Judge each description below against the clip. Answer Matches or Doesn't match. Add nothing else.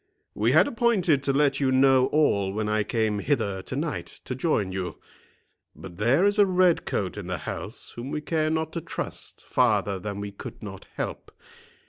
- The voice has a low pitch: Matches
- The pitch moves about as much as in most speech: Doesn't match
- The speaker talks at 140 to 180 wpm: Doesn't match